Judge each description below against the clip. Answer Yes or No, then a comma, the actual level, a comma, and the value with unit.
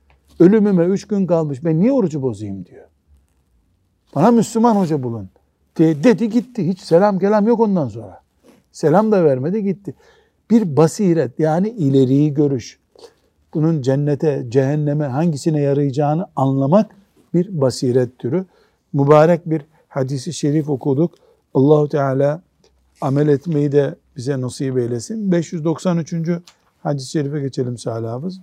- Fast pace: No, average, 120 wpm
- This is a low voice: No, medium, 155 Hz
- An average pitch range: Yes, average, 4.7 semitones